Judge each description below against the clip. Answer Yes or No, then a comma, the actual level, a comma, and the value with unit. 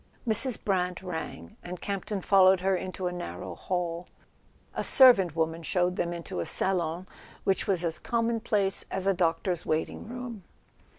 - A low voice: No, medium, 185 Hz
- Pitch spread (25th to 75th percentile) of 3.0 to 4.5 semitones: No, narrow, 2.4 semitones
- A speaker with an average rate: Yes, average, 160 wpm